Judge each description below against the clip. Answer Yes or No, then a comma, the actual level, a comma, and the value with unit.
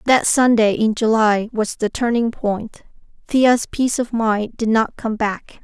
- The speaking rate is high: No, average, 170 wpm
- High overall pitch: Yes, high, 225 Hz